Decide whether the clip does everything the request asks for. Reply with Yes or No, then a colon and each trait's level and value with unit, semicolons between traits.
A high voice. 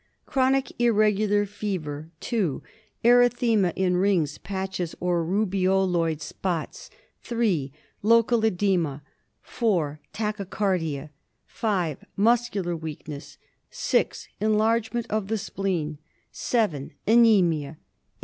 Yes: high, 195 Hz